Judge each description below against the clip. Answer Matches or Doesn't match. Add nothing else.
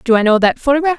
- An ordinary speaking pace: Doesn't match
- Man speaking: Doesn't match